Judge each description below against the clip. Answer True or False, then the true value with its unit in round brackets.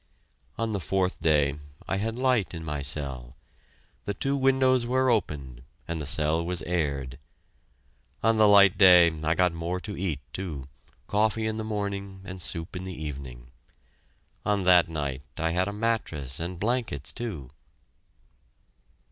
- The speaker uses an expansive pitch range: True (5.9 semitones)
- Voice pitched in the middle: False (90 Hz)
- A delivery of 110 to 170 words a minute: True (155 wpm)